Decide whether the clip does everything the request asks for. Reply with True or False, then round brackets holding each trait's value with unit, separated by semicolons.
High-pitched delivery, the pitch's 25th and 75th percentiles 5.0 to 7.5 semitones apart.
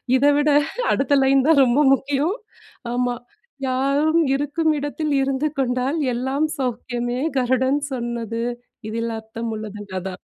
False (260 Hz; 3.2 semitones)